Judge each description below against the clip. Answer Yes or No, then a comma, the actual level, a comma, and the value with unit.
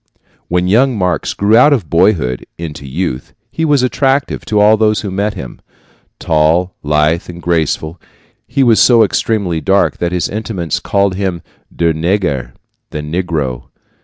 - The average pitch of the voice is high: No, very low, 90 Hz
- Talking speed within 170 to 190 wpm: No, average, 155 wpm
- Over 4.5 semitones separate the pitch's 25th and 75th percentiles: Yes, average, 5.1 semitones